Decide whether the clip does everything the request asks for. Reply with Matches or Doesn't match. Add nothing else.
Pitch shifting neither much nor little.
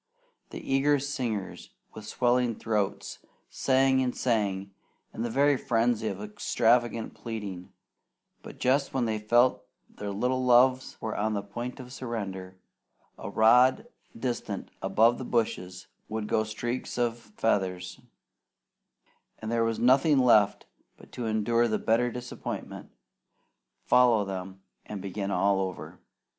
Matches